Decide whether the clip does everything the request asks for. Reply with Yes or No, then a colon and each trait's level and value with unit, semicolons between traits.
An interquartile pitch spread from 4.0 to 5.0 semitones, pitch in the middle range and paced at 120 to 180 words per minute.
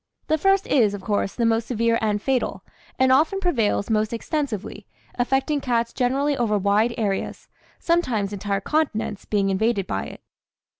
No: average, 4.5 semitones; high, 230 Hz; average, 155 wpm